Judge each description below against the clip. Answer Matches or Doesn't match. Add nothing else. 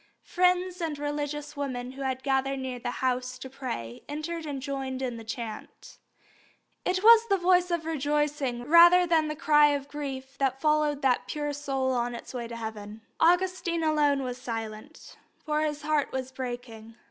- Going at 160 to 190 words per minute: Matches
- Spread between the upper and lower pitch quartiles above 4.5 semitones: Doesn't match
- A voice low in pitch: Doesn't match